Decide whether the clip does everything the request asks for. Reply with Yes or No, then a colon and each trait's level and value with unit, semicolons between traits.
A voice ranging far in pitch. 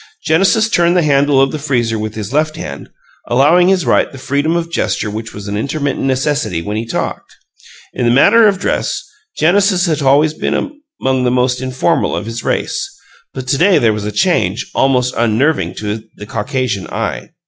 Yes: wide, 5.7 semitones